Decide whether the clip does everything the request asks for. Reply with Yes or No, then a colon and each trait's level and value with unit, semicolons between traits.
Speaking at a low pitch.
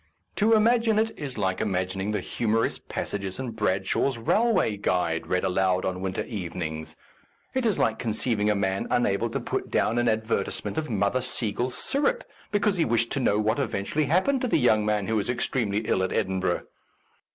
Yes: low, 110 Hz